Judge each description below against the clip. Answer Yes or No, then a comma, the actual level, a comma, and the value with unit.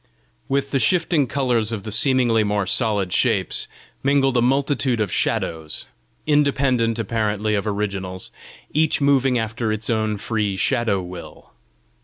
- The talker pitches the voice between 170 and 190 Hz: No, low, 115 Hz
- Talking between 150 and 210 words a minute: No, slow, 135 wpm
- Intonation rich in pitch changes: No, average, 4.5 semitones